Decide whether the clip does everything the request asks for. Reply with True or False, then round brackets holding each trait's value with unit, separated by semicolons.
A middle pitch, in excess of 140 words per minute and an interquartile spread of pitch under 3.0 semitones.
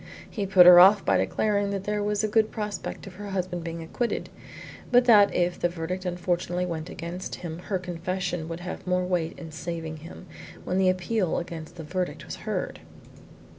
True (180 Hz; 190 wpm; 2.6 semitones)